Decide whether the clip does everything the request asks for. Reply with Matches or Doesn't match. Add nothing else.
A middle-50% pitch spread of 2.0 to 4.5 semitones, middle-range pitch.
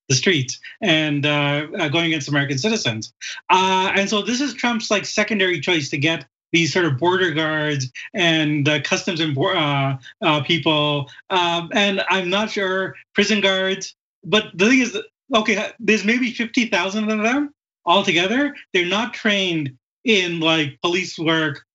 Doesn't match